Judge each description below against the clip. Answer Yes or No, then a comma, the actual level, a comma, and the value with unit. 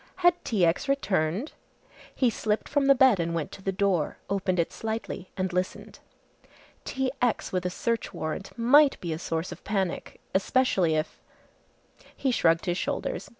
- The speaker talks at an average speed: Yes, average, 165 wpm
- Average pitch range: No, wide, 6.0 semitones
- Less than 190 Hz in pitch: No, high, 195 Hz